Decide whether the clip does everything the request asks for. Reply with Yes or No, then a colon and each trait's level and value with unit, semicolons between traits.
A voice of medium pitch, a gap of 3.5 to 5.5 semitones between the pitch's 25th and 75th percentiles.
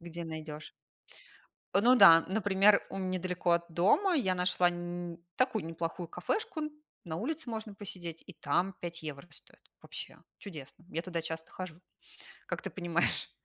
No: medium, 175 Hz; average, 3.0 semitones